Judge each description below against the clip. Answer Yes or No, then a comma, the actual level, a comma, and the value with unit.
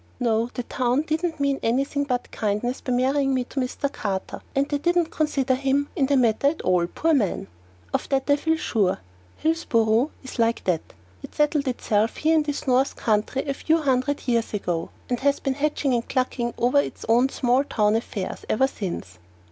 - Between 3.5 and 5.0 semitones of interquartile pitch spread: Yes, average, 3.8 semitones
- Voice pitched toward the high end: Yes, very high, 260 Hz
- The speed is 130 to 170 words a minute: No, average, 190 wpm